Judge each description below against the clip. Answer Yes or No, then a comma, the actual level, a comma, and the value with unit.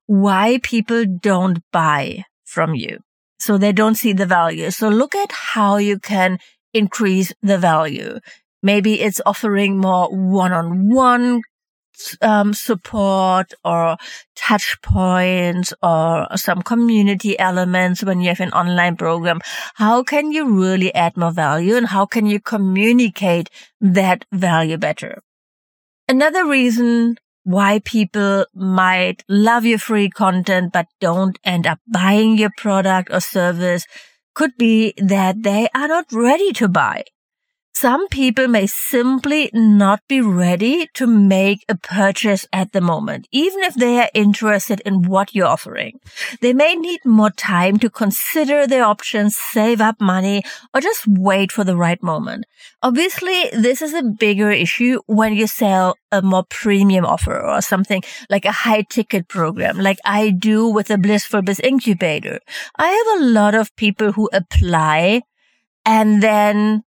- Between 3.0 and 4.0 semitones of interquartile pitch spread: Yes, average, 3.6 semitones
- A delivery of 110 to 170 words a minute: Yes, average, 145 wpm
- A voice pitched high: Yes, high, 205 Hz